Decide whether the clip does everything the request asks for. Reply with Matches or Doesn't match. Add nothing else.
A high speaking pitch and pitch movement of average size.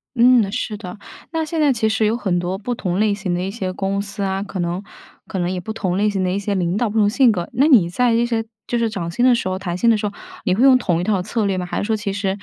Matches